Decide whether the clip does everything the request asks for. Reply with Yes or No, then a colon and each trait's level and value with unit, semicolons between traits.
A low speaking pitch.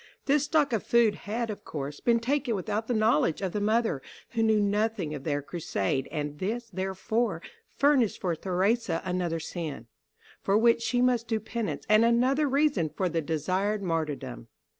No: high, 210 Hz